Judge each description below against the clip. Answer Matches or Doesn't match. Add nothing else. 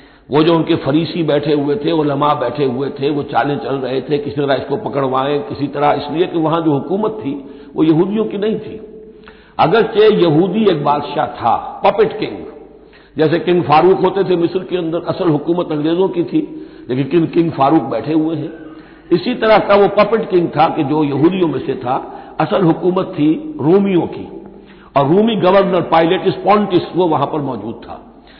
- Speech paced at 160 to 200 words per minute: Matches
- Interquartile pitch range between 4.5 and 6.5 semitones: Matches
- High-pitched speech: Doesn't match